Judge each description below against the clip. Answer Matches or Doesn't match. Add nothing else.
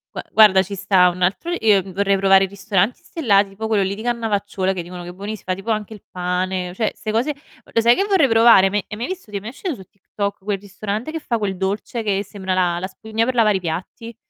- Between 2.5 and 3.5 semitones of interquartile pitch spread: Matches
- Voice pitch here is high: Matches